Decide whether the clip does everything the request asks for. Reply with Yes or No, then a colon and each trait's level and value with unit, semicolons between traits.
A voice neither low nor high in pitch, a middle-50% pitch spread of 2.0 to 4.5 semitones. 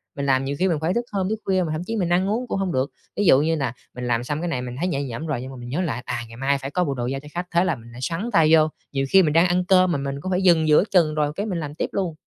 No: medium, 155 Hz; average, 5.0 semitones